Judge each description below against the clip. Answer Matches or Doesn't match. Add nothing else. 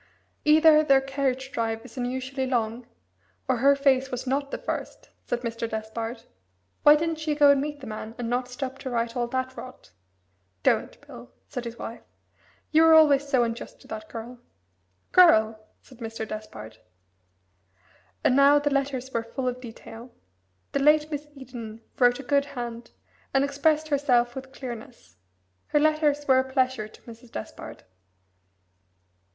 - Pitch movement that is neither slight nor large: Matches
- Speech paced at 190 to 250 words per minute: Doesn't match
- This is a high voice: Matches